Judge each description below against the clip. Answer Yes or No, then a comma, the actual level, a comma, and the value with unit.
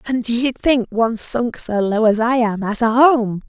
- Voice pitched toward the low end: No, high, 230 Hz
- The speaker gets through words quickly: Yes, fast, 240 wpm